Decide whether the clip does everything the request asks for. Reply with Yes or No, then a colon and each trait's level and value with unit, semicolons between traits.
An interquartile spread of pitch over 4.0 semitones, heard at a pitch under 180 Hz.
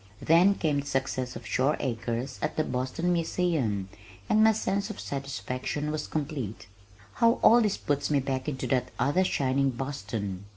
Yes: average, 4.6 semitones; medium, 140 Hz